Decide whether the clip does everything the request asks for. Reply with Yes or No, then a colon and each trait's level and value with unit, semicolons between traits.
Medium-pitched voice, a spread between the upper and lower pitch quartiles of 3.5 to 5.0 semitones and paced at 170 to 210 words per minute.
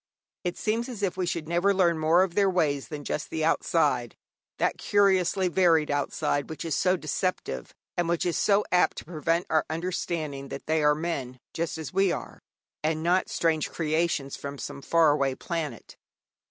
No: medium, 165 Hz; average, 3.0 semitones; average, 180 wpm